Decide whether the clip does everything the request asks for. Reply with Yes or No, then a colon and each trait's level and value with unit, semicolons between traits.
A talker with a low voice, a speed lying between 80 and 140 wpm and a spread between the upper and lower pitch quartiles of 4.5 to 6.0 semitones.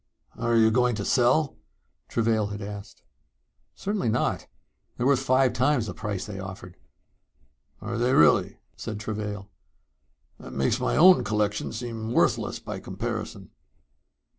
No: low, 110 Hz; slow, 135 wpm; average, 3.3 semitones